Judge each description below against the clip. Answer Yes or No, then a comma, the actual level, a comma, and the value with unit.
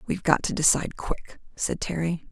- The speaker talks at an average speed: Yes, average, 180 wpm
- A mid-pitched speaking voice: Yes, medium, 165 Hz